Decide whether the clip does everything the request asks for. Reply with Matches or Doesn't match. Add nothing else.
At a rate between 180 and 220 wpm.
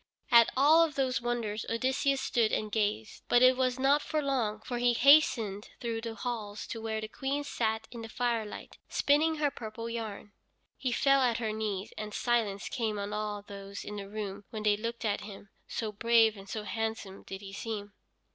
Matches